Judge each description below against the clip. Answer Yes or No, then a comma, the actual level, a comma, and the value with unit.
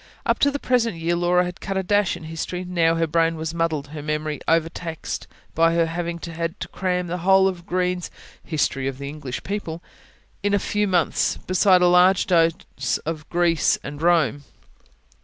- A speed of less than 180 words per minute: No, average, 185 wpm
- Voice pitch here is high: No, medium, 170 Hz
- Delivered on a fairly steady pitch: Yes, narrow, 2.1 semitones